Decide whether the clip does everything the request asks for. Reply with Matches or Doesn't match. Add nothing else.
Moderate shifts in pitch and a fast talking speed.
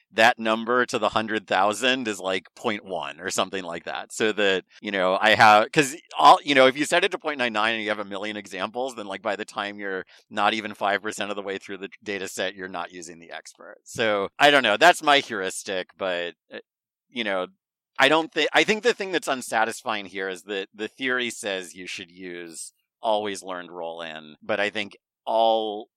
Matches